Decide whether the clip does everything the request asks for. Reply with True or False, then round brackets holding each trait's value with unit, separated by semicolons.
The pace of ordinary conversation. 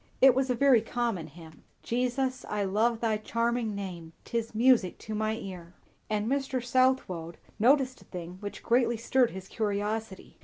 True (160 wpm)